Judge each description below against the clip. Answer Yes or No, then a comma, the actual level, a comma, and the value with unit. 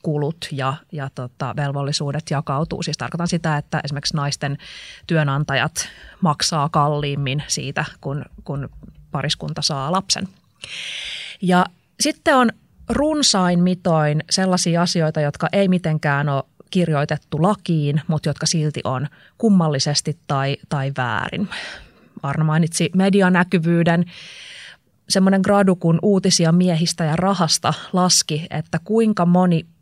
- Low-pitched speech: No, medium, 160 Hz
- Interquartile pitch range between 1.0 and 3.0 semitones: No, average, 3.7 semitones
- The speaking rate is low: No, average, 115 wpm